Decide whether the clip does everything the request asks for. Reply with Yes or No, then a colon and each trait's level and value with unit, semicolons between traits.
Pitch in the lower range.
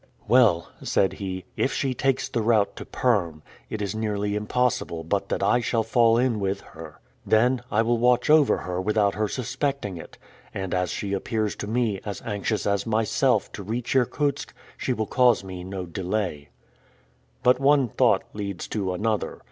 Yes: low, 110 Hz